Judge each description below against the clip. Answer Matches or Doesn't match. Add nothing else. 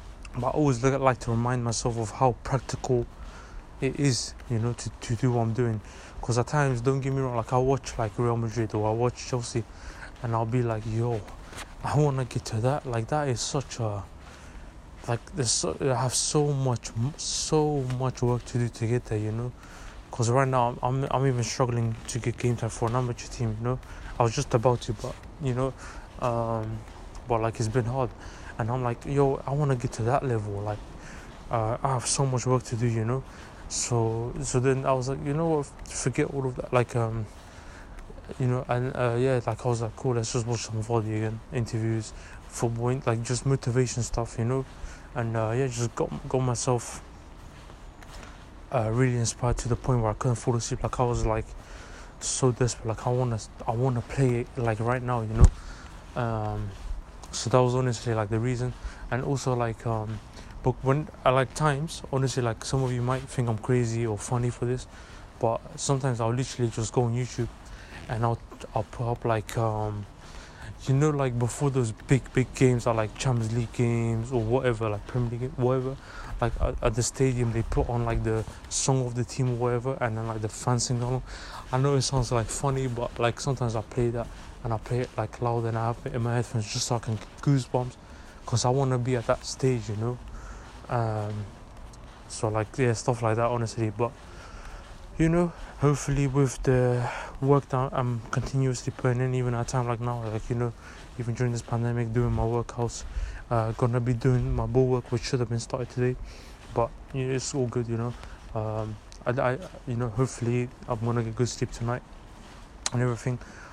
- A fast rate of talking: Matches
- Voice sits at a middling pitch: Doesn't match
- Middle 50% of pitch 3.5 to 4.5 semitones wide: Doesn't match